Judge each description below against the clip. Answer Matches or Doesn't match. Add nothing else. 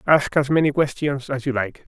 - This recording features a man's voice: Matches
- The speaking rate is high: Matches